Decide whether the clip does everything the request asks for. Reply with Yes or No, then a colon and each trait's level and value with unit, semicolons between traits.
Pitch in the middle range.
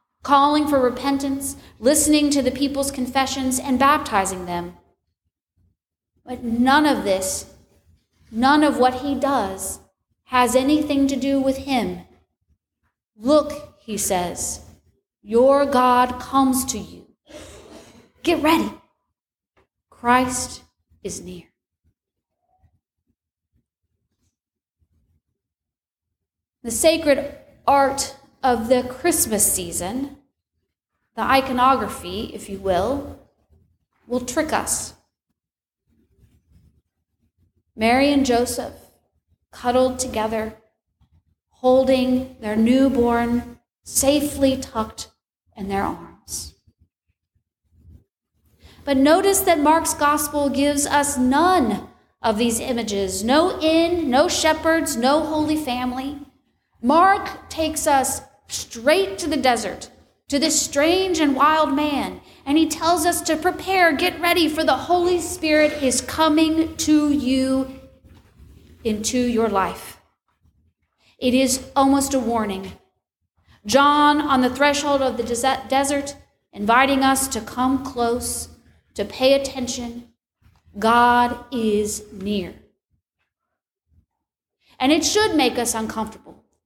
No: very high, 255 Hz